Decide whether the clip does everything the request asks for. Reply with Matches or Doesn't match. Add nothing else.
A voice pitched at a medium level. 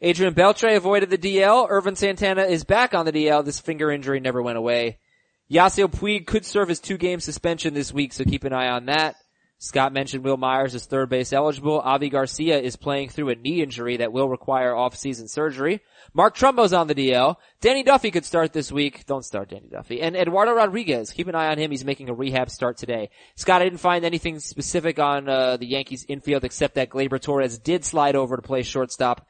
Matches